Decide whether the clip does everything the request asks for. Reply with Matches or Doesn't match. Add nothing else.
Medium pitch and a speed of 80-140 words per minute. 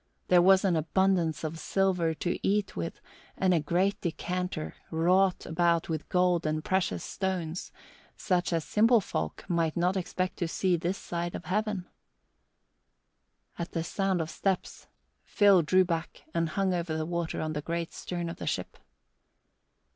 Doesn't match